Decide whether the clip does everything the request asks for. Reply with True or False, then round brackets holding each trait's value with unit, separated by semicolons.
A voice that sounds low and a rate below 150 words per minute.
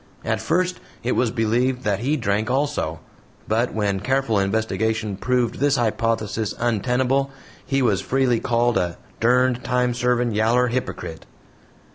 True (120 Hz; 135 wpm)